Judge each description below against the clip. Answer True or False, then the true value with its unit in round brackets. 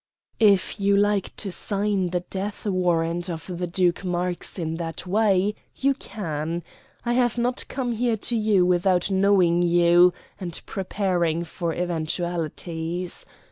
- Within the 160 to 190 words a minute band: False (140 wpm)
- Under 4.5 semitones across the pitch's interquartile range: True (2.9 semitones)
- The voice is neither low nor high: True (180 Hz)